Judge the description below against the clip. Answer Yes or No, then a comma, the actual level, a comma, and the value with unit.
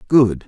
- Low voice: Yes, low, 115 Hz